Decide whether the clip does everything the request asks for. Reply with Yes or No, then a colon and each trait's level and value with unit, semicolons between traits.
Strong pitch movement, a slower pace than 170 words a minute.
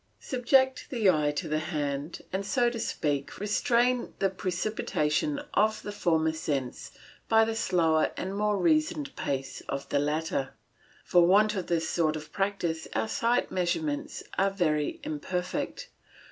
Yes: wide, 6.6 semitones; average, 145 wpm